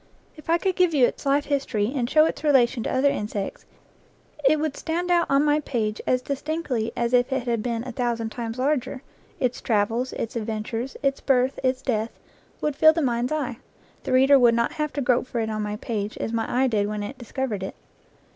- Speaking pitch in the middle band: No, very high, 255 Hz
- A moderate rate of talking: No, fast, 215 wpm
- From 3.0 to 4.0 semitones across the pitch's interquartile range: Yes, average, 3.7 semitones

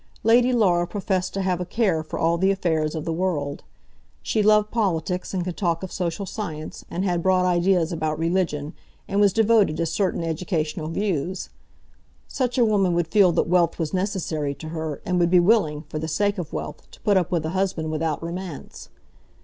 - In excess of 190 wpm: Yes, average, 200 wpm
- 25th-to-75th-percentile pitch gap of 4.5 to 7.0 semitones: No, average, 3.4 semitones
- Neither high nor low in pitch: Yes, medium, 175 Hz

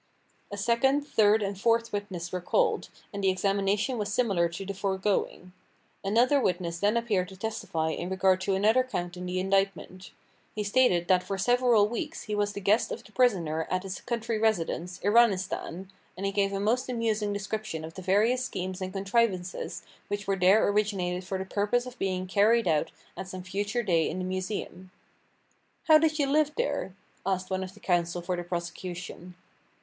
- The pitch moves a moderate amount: Yes, average, 3.2 semitones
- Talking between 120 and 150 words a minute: No, average, 185 wpm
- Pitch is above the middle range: Yes, high, 195 Hz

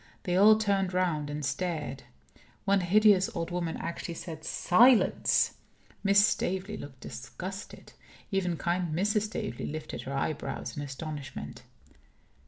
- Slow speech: Yes, slow, 125 wpm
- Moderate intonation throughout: Yes, average, 4.6 semitones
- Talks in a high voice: No, medium, 175 Hz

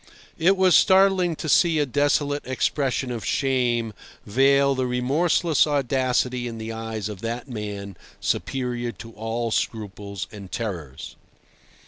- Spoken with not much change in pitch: No, average, 4.2 semitones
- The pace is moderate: No, slow, 130 wpm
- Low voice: Yes, low, 125 Hz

